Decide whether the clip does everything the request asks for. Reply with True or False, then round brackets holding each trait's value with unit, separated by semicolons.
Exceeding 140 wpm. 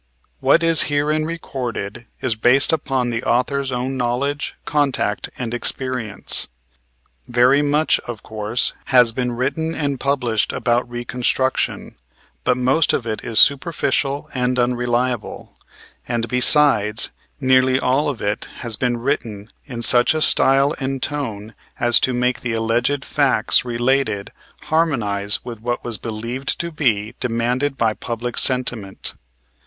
False (135 wpm)